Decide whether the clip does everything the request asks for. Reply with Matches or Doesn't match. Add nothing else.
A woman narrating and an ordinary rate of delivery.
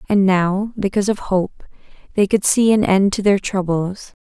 Matches